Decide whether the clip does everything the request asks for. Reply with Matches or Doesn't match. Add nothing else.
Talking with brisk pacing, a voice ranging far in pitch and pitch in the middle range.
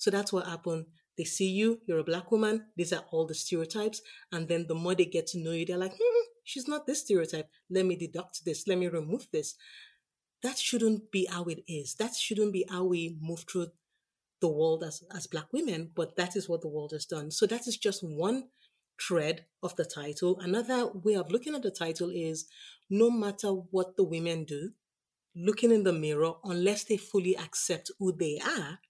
Doesn't match